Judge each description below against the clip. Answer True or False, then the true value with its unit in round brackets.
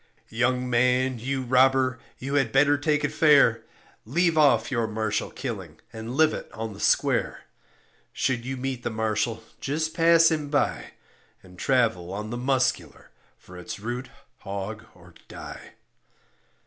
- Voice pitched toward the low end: True (125 Hz)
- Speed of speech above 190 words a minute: False (145 wpm)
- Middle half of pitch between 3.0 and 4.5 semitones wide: True (3.8 semitones)